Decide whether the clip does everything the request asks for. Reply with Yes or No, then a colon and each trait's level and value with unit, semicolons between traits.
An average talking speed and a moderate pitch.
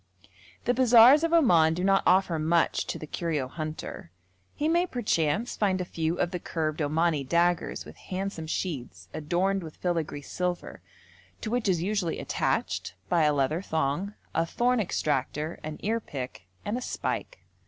Yes: average, 160 wpm; medium, 170 Hz